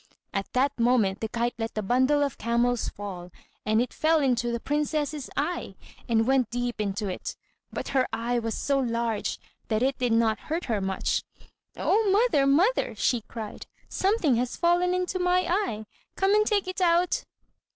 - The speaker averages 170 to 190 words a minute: Yes, average, 175 wpm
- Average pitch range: No, wide, 6.9 semitones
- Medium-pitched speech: No, very high, 250 Hz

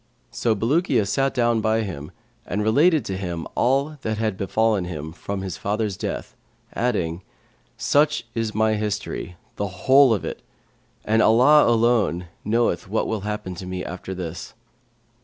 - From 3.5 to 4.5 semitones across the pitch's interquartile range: Yes, average, 4.0 semitones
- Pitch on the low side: Yes, low, 110 Hz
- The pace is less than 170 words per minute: Yes, average, 155 wpm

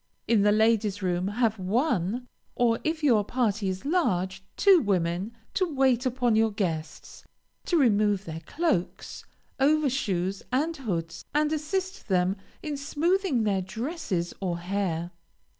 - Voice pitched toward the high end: Yes, high, 220 Hz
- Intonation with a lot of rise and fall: Yes, wide, 7.1 semitones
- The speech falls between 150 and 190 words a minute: No, slow, 135 wpm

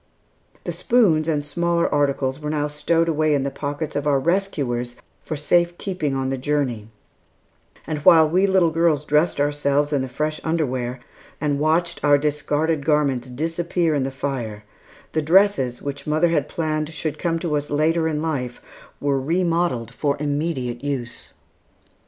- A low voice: No, medium, 150 Hz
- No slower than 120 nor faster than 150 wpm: No, average, 160 wpm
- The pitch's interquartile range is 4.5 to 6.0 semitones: No, average, 2.9 semitones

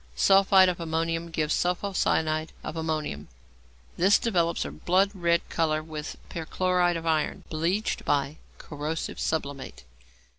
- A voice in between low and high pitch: Yes, medium, 165 Hz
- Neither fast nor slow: No, slow, 125 wpm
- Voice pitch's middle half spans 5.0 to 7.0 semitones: No, narrow, 2.5 semitones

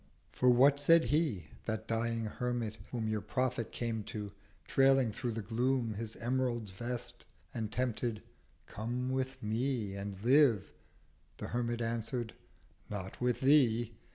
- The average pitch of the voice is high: No, low, 120 Hz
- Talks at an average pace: No, slow, 130 wpm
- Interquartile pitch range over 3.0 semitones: No, narrow, 2.6 semitones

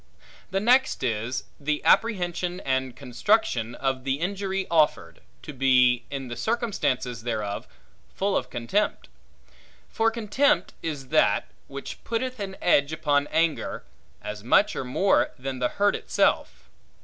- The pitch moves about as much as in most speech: No, wide, 7.6 semitones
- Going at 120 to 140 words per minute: Yes, slow, 135 wpm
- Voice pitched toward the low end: No, medium, 145 Hz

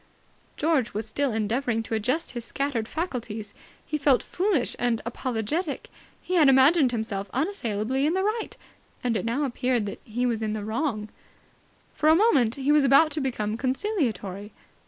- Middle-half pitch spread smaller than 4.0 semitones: No, average, 5.1 semitones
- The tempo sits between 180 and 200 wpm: No, average, 165 wpm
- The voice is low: No, very high, 250 Hz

